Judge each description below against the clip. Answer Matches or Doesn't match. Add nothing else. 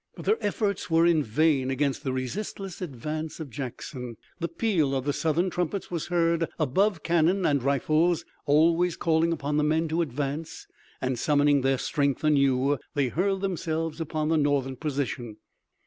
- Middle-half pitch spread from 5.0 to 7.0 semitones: Doesn't match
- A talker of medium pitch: Matches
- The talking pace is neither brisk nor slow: Matches